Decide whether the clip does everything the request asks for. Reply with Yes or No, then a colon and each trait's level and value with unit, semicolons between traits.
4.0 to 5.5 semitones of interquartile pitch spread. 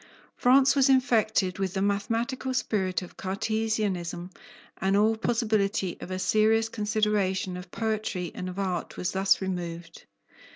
No: average, 3.1 semitones